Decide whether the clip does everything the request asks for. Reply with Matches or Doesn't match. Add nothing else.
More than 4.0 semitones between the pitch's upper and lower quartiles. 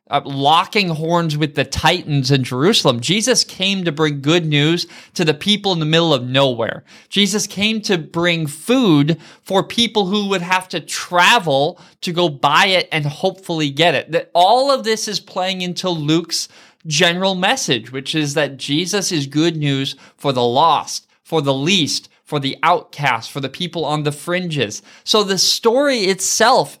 Matches